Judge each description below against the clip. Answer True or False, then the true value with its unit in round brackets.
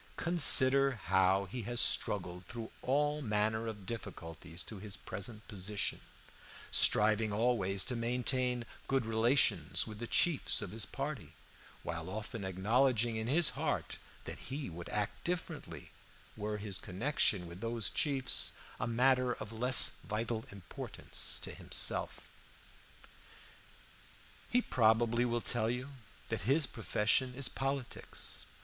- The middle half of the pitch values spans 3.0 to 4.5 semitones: True (3.6 semitones)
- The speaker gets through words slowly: True (130 wpm)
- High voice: False (115 Hz)